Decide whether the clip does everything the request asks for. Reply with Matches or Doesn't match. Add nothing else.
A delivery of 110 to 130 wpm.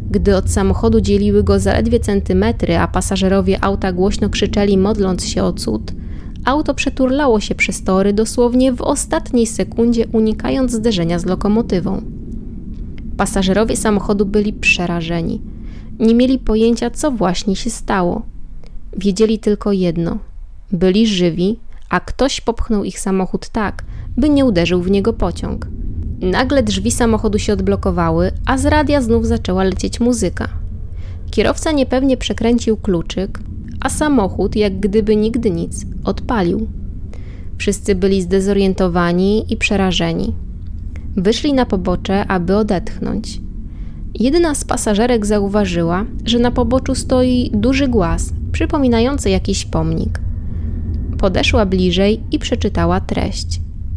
Matches